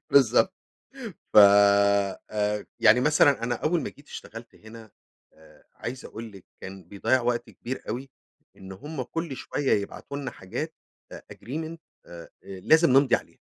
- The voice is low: Yes, low, 115 Hz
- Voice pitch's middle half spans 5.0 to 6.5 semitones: Yes, wide, 5.6 semitones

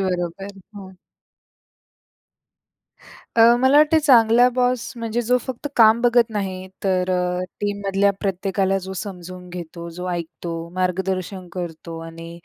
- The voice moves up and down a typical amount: Yes, average, 4.1 semitones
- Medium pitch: No, high, 195 Hz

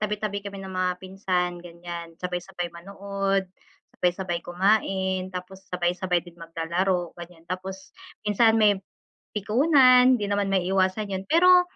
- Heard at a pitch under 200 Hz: Yes, high, 190 Hz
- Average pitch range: No, narrow, 2.3 semitones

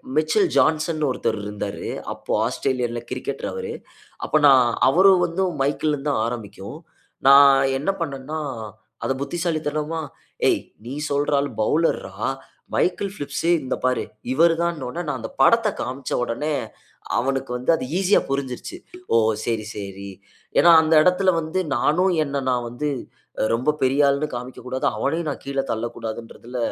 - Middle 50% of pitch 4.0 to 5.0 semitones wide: Yes, average, 4.5 semitones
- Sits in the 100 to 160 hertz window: Yes, medium, 140 Hz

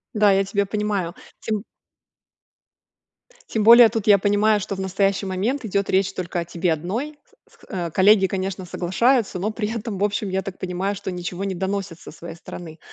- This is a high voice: Yes, high, 195 Hz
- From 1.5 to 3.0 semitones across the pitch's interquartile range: Yes, narrow, 2.4 semitones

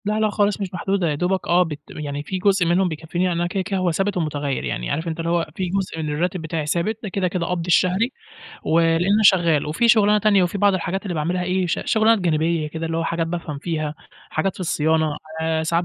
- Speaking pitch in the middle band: Yes, medium, 175 Hz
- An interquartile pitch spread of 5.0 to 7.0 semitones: No, average, 3.0 semitones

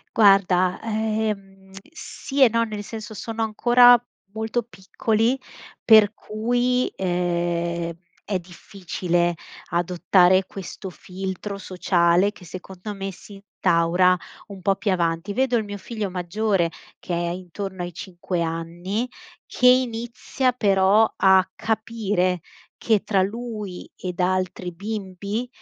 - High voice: Yes, high, 195 Hz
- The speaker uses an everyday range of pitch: Yes, average, 3.5 semitones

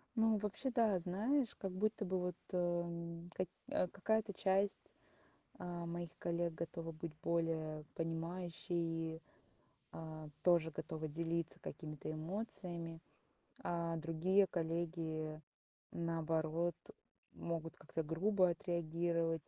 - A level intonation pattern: Yes, narrow, 1.9 semitones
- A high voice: No, medium, 170 Hz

